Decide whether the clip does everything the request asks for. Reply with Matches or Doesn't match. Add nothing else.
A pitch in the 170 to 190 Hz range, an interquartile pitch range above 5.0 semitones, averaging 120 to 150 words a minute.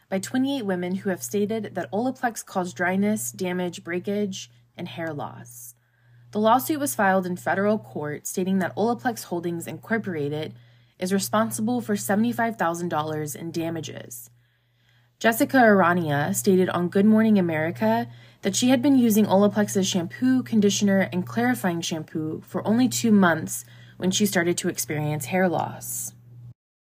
Matches